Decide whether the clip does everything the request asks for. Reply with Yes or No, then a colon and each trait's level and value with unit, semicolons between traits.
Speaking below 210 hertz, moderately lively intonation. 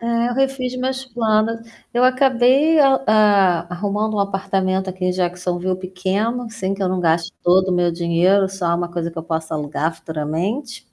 Yes: high, 190 Hz; average, 4.9 semitones